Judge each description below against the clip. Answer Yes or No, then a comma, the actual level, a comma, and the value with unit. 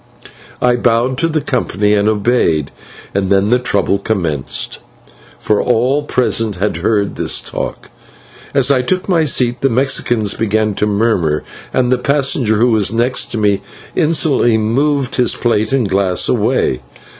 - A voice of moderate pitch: No, low, 115 Hz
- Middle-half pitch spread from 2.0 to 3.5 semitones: No, average, 3.9 semitones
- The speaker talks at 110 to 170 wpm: Yes, average, 155 wpm